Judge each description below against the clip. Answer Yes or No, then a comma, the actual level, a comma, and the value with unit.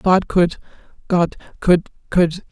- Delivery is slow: Yes, slow, 70 wpm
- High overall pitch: No, medium, 175 Hz